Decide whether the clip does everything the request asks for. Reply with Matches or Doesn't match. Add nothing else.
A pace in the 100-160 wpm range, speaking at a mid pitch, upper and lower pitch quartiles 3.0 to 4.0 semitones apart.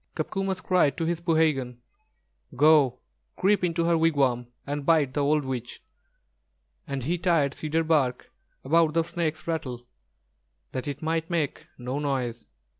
Matches